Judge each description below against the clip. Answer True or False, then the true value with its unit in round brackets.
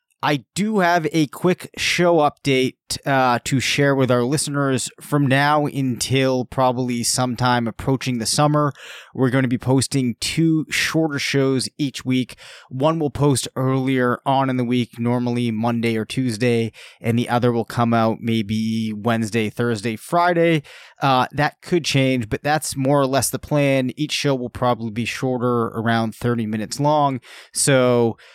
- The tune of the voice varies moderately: True (3.1 semitones)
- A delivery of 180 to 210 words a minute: False (160 wpm)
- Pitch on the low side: True (130 Hz)